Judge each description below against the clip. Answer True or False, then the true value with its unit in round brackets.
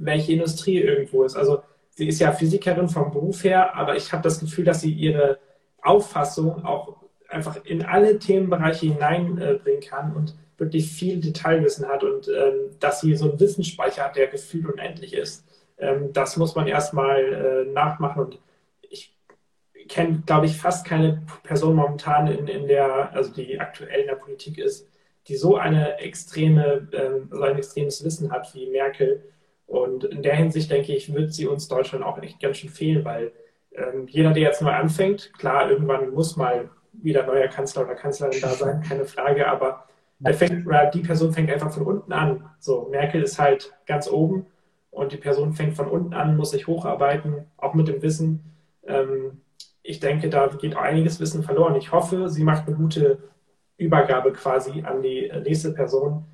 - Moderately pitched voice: True (155 Hz)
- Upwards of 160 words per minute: True (180 wpm)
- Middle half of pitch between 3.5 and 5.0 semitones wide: True (4.1 semitones)